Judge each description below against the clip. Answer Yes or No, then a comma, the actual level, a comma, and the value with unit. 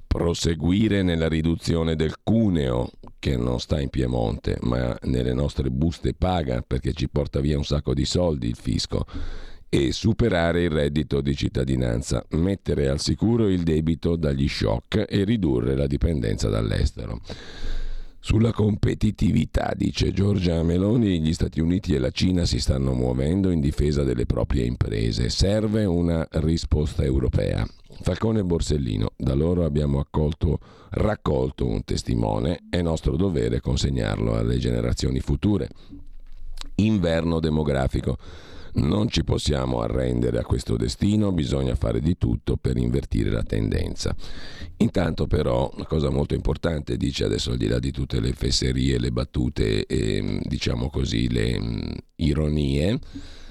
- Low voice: Yes, very low, 80 Hz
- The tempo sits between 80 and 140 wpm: Yes, average, 135 wpm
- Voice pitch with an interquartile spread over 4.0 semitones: Yes, average, 5.1 semitones